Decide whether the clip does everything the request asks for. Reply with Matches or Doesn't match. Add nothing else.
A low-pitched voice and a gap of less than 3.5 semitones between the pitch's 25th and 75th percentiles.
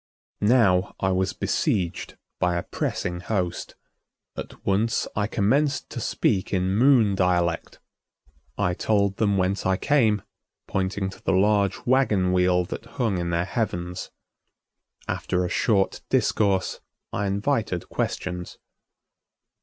Matches